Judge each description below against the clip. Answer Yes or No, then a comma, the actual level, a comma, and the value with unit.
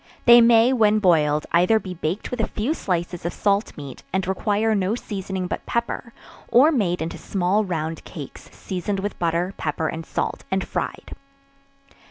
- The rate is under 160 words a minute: No, average, 170 wpm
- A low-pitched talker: No, high, 190 Hz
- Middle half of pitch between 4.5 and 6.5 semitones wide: No, average, 4.1 semitones